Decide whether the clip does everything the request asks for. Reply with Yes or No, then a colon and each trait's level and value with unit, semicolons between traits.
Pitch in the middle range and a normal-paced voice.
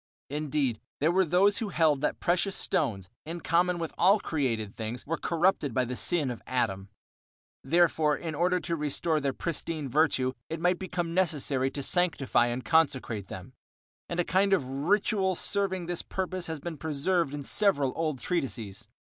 Yes: medium, 160 Hz; average, 170 wpm